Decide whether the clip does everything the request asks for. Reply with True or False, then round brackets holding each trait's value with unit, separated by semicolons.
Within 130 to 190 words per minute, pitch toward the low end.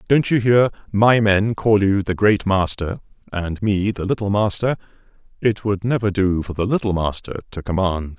True (185 wpm; 100 Hz)